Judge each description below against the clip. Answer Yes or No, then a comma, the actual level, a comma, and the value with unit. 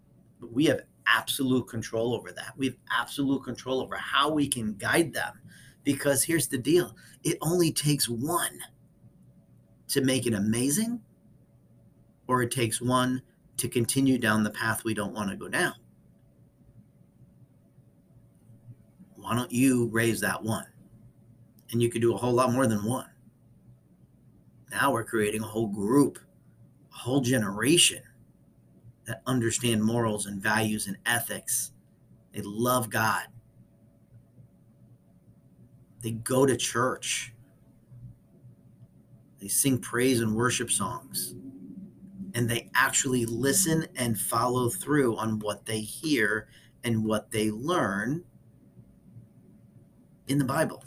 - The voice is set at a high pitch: No, low, 120 Hz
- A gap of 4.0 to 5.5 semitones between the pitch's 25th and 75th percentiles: No, average, 2.8 semitones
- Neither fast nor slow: No, slow, 125 wpm